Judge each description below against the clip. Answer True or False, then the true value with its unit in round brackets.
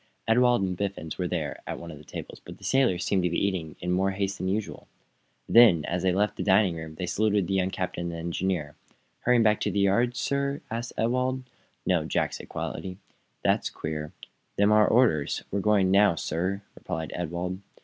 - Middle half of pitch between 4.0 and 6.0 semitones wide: False (3.6 semitones)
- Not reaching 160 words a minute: False (200 wpm)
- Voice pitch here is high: False (95 Hz)